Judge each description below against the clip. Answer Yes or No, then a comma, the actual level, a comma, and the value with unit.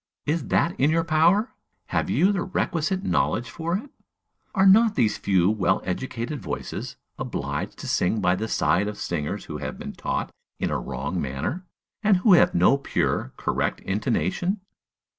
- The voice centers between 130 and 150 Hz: Yes, medium, 140 Hz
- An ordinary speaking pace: Yes, average, 165 wpm